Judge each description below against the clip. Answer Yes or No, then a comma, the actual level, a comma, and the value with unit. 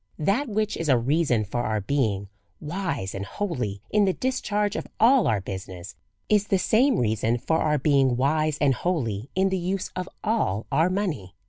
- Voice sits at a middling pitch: Yes, medium, 150 Hz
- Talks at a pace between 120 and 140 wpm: No, average, 190 wpm